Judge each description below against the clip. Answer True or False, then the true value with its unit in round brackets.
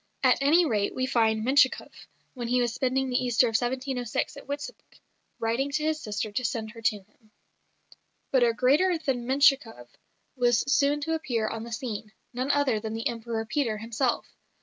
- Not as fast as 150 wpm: False (180 wpm)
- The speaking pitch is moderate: False (245 Hz)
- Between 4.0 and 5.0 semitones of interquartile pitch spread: False (3.5 semitones)